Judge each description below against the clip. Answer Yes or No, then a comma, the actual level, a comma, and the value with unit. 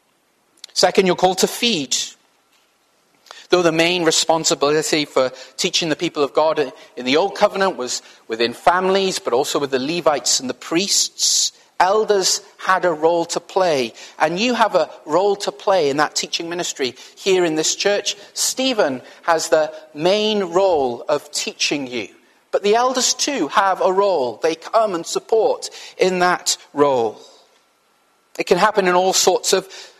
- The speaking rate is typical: Yes, average, 160 wpm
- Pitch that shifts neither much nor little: Yes, average, 4.5 semitones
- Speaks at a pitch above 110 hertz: Yes, medium, 185 Hz